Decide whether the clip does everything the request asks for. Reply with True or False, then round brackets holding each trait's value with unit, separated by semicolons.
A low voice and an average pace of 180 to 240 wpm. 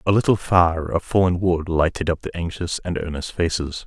True (85 Hz; 200 wpm)